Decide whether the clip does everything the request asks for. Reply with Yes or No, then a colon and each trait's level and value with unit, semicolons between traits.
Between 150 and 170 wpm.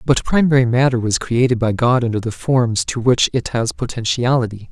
No: average, 190 wpm